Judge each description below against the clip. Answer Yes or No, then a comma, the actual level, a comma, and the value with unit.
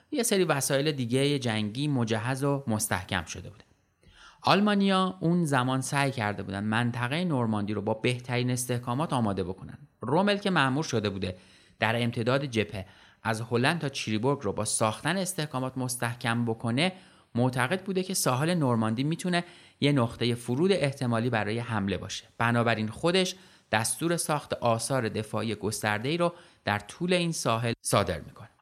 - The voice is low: Yes, low, 125 Hz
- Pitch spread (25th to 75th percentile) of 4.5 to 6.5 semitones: Yes, wide, 5.4 semitones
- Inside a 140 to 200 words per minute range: Yes, average, 145 wpm